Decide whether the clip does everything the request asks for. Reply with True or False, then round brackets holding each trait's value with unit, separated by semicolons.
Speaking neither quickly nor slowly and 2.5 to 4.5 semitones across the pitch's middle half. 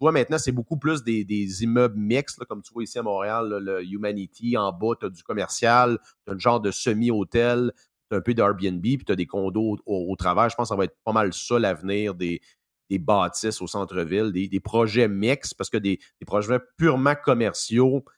False (230 wpm; 3.5 semitones)